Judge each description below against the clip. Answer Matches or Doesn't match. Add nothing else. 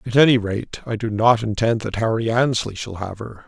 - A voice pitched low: Matches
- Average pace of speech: Doesn't match